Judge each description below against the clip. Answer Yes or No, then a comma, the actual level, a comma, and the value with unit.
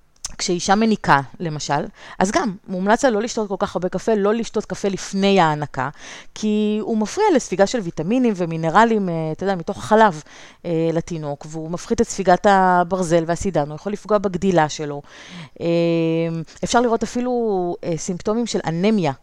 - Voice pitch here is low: No, high, 190 Hz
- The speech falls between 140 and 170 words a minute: Yes, average, 145 wpm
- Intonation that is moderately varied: Yes, average, 4.4 semitones